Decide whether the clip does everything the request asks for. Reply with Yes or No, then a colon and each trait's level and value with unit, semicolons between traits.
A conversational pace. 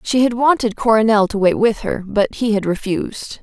No: fast, 210 wpm